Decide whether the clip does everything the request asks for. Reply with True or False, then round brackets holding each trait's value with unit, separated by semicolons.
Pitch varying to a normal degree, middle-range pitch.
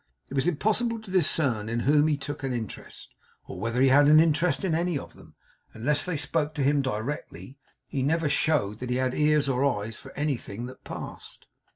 True (3.6 semitones; 145 Hz)